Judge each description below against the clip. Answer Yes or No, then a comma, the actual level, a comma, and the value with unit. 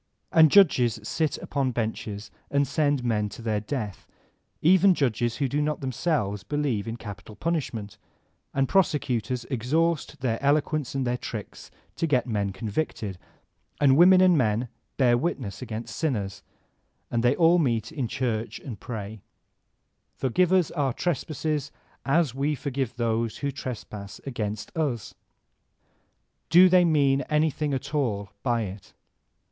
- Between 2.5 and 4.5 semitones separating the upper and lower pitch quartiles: No, average, 5.3 semitones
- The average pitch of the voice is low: Yes, low, 130 Hz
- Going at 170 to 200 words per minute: No, average, 150 wpm